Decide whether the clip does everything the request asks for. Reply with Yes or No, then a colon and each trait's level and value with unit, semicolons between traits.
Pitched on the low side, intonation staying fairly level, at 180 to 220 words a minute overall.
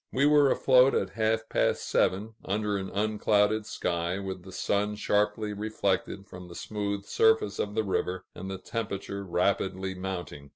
No: low, 100 Hz; narrow, 2.3 semitones; average, 160 wpm